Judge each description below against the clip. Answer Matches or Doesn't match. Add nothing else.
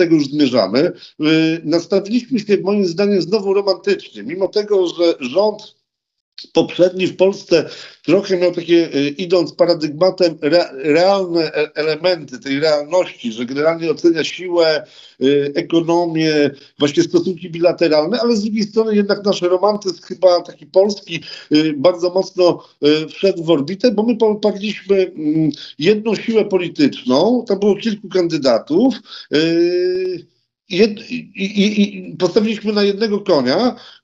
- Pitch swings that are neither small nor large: Matches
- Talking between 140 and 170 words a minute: Doesn't match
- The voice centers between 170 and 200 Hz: Matches